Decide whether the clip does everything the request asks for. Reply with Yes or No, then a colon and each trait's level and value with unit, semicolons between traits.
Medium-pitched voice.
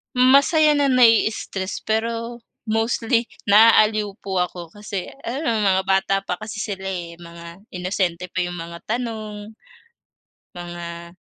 No: high, 210 Hz